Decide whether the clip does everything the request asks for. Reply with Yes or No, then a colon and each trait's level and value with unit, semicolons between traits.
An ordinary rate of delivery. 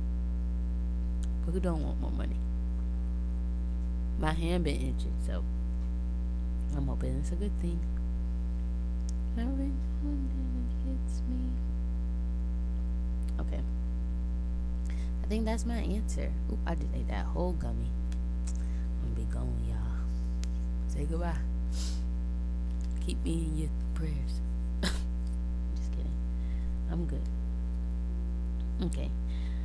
No: slow, 95 wpm